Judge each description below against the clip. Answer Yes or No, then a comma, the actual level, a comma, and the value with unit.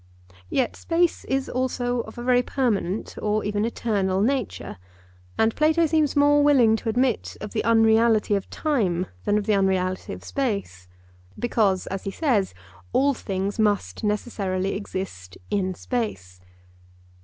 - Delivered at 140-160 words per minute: Yes, average, 145 wpm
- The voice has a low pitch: No, high, 220 Hz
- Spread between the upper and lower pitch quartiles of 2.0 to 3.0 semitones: No, average, 4.6 semitones